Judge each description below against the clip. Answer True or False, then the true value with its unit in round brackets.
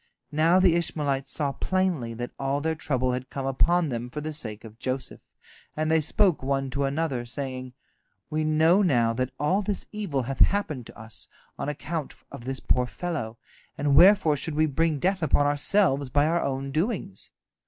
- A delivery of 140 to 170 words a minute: False (185 wpm)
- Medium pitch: True (145 Hz)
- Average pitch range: True (4.0 semitones)